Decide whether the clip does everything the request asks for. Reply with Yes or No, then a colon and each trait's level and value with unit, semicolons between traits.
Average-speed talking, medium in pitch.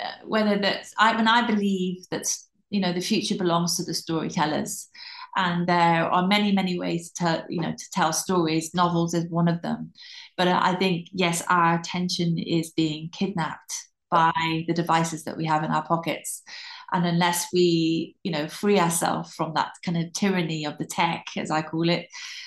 Yes: average, 185 wpm; medium, 175 Hz